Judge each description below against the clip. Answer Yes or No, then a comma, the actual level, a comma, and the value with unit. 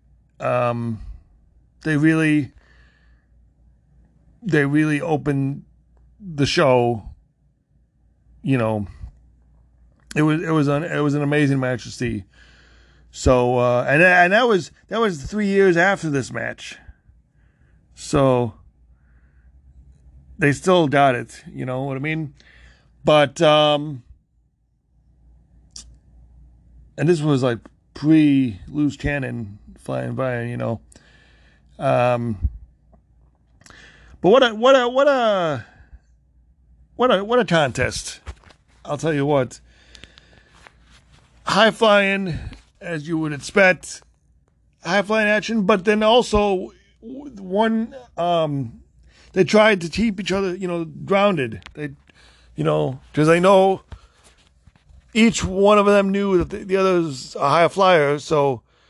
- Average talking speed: No, slow, 120 wpm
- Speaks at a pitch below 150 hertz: Yes, medium, 140 Hz